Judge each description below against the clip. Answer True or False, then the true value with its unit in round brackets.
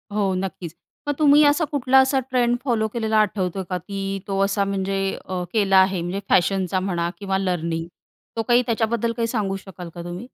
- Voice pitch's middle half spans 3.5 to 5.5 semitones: True (3.9 semitones)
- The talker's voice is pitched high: True (195 Hz)